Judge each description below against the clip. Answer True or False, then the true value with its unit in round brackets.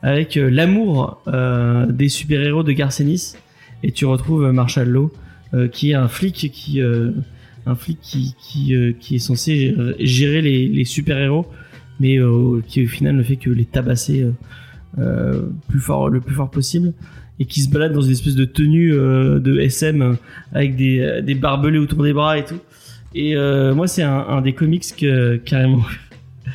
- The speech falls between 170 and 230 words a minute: True (190 wpm)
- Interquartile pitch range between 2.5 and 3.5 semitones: True (2.8 semitones)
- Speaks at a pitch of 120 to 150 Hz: True (135 Hz)